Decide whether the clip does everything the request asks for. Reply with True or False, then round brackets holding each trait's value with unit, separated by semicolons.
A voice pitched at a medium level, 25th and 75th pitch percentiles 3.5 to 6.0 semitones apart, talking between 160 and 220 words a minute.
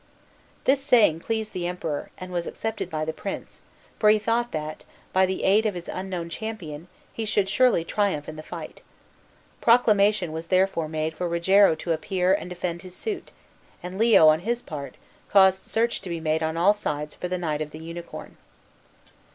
True (180 Hz; 4.4 semitones; 185 wpm)